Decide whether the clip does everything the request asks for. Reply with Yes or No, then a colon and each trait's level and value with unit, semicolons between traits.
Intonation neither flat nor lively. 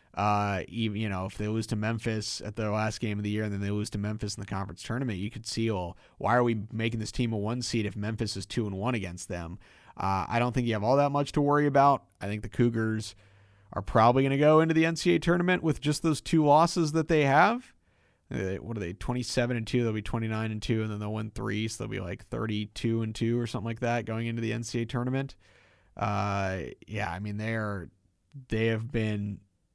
Yes: average, 3.1 semitones